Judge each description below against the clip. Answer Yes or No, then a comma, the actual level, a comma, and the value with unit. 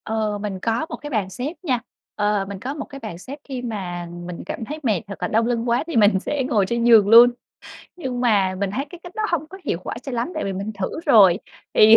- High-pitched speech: Yes, high, 225 Hz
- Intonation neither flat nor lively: Yes, average, 4.5 semitones